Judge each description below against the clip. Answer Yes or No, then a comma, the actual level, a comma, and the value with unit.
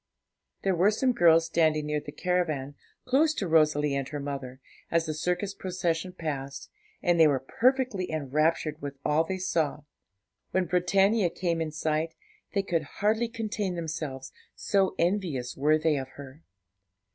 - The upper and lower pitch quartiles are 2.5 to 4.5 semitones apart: Yes, average, 3.9 semitones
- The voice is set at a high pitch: No, medium, 165 Hz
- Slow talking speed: No, average, 155 wpm